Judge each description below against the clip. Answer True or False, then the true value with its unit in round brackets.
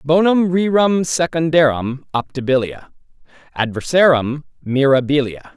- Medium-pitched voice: True (145 Hz)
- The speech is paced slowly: True (65 wpm)